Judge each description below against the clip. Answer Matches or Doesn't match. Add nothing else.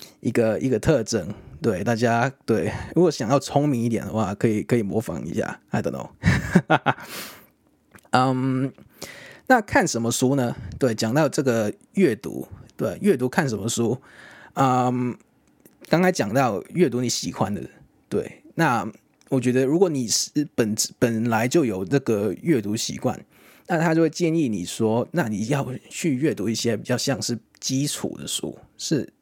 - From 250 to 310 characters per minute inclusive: Doesn't match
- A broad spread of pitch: Doesn't match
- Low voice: Matches